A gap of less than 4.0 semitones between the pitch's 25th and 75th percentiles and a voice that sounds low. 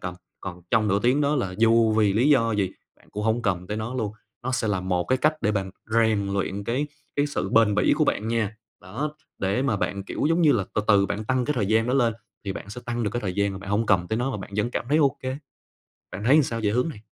Yes: average, 3.6 semitones; low, 110 Hz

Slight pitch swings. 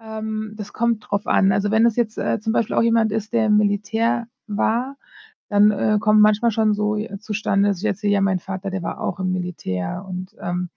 Yes: narrow, 1.9 semitones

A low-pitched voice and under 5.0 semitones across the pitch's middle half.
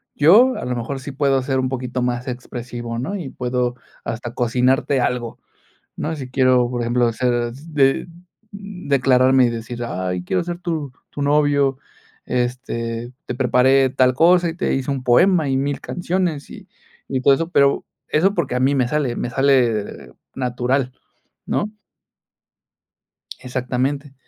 Yes: low, 130 Hz; average, 2.7 semitones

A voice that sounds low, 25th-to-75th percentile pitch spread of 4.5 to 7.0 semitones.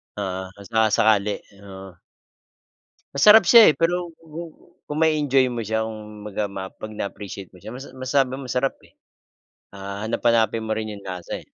Yes: low, 110 Hz; average, 5.2 semitones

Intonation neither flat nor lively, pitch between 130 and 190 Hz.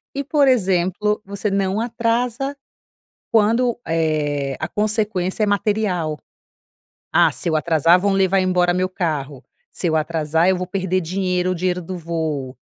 Yes: average, 4.2 semitones; medium, 185 Hz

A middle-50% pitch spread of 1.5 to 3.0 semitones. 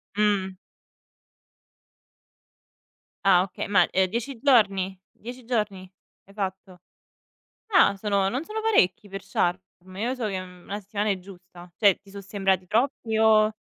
Yes: average, 2.7 semitones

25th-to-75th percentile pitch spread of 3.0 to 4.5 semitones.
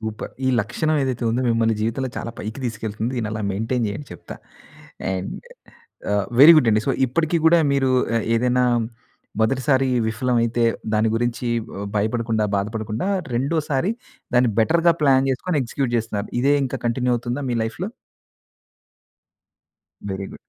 Yes: average, 3.3 semitones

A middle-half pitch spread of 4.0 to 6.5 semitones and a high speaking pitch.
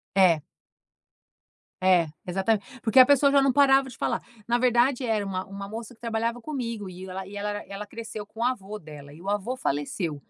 Yes: average, 4.3 semitones; high, 215 Hz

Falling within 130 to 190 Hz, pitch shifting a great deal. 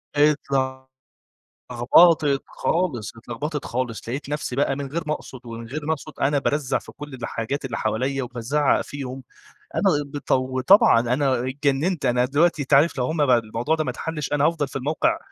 No: medium, 140 Hz; average, 3.1 semitones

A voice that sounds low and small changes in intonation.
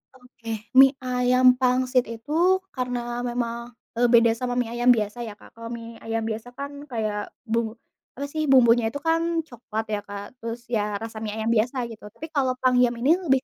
No: high, 240 Hz; narrow, 2.0 semitones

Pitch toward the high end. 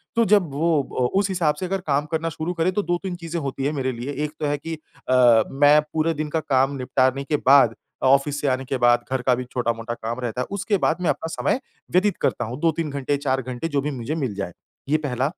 No: medium, 145 Hz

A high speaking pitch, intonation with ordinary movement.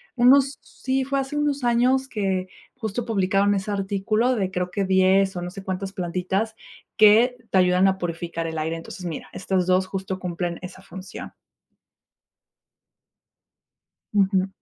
Yes: high, 195 Hz; average, 3.5 semitones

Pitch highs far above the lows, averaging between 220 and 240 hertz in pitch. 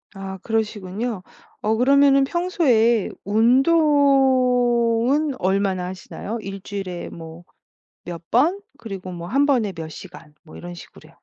Yes: wide, 6.3 semitones; high, 225 Hz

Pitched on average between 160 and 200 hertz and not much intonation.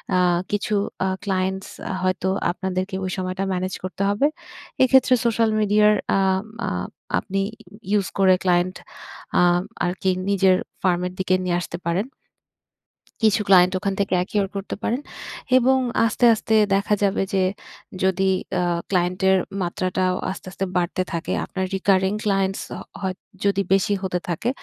Yes: high, 190 Hz; narrow, 1.5 semitones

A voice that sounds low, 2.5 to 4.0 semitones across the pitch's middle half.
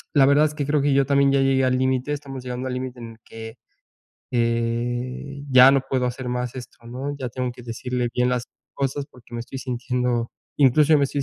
No: low, 130 Hz; narrow, 2.0 semitones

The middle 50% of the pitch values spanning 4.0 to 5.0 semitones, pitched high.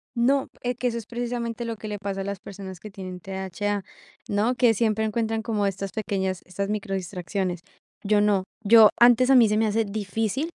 No: average, 2.9 semitones; high, 210 Hz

